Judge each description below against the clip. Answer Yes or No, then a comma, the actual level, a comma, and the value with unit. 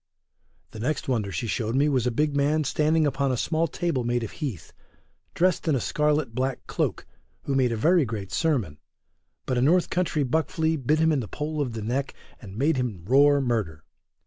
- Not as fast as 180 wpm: No, fast, 205 wpm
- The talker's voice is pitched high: No, low, 135 Hz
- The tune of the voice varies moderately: Yes, average, 4.7 semitones